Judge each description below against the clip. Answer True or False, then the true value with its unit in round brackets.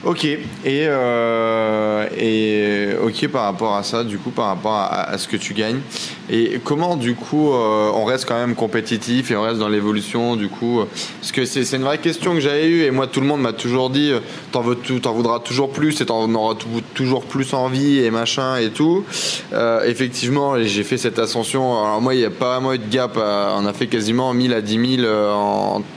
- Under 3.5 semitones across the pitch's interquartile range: True (3.0 semitones)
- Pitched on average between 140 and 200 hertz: False (120 Hz)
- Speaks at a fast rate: True (225 wpm)